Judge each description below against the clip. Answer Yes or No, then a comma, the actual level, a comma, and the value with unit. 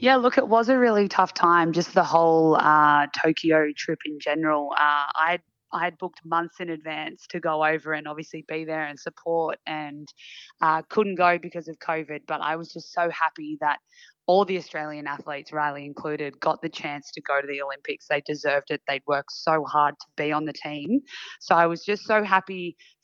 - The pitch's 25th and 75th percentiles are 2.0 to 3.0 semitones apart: Yes, narrow, 2.4 semitones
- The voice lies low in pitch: No, medium, 155 Hz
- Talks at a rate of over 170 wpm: Yes, fast, 205 wpm